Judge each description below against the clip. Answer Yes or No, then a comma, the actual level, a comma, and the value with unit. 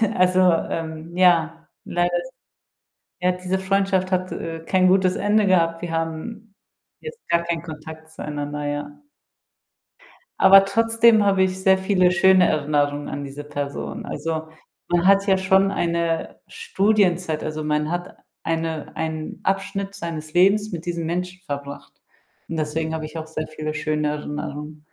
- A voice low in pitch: No, medium, 170 Hz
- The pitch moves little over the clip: No, average, 3.4 semitones